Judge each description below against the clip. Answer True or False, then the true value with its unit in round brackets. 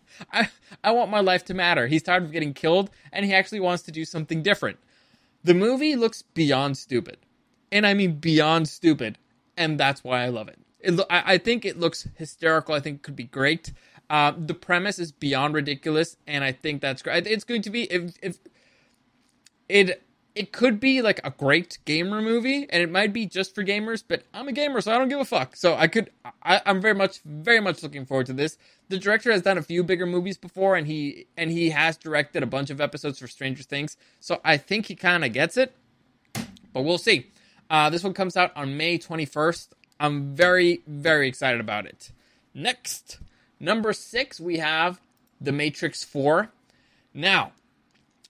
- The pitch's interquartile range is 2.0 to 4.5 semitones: False (5.0 semitones)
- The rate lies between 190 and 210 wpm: True (200 wpm)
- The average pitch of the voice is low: False (170 Hz)